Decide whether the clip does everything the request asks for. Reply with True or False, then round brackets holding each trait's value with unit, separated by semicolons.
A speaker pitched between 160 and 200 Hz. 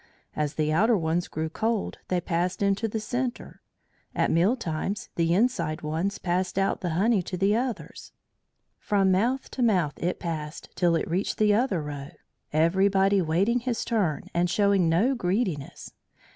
True (185 Hz)